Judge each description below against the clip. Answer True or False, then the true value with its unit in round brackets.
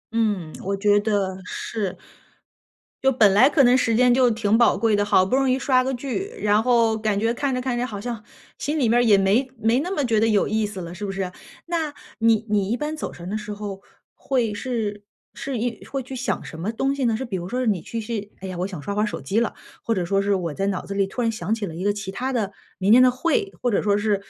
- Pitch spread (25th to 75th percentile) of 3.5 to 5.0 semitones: True (3.9 semitones)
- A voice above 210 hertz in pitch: True (220 Hz)